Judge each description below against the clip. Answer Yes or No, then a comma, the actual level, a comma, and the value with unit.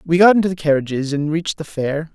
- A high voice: No, medium, 160 Hz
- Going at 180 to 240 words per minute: No, fast, 250 wpm